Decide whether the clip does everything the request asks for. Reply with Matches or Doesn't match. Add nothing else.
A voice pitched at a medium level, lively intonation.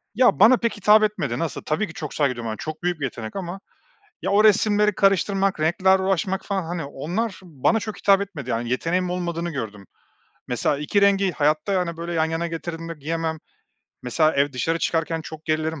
Doesn't match